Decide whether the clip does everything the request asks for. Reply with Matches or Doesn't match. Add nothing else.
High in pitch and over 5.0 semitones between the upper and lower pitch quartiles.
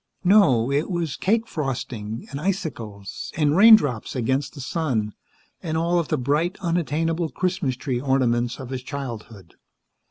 Doesn't match